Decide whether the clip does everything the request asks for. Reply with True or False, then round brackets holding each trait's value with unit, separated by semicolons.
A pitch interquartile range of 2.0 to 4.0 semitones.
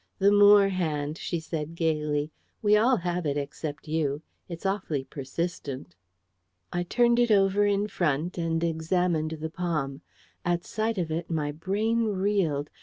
False (4.5 semitones)